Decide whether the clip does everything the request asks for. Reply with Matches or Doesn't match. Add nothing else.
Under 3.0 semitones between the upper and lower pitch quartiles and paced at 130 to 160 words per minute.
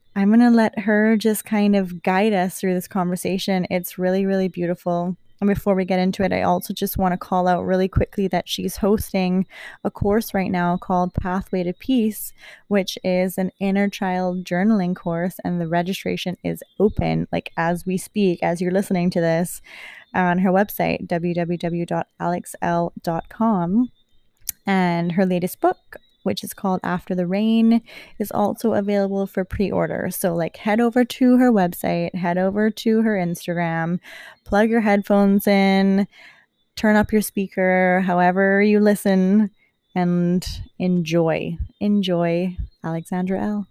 Matches